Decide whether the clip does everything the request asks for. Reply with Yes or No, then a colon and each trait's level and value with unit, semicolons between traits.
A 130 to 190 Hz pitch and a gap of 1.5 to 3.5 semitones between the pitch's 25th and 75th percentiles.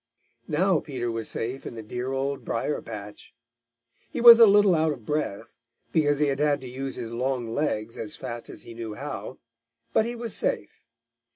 No: low, 135 Hz; average, 4.7 semitones